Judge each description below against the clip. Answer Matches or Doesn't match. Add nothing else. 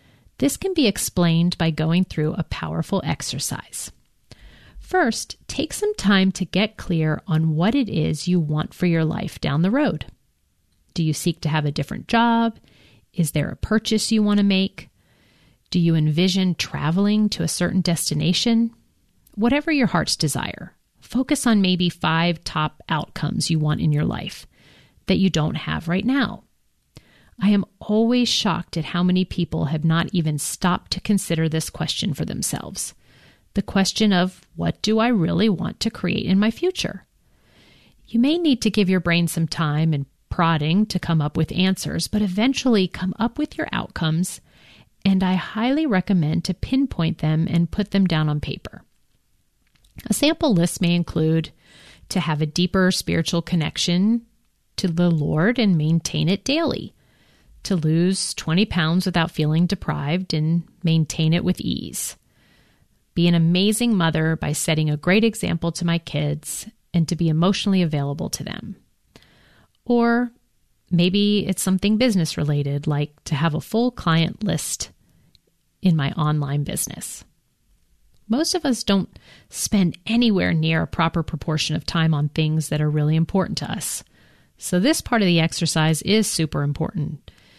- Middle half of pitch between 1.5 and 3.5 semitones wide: Doesn't match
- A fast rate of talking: Doesn't match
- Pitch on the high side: Doesn't match